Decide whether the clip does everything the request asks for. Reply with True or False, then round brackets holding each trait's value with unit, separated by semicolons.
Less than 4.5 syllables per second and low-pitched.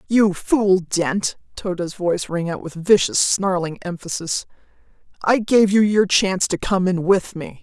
False (4.3 syllables/s; 185 Hz)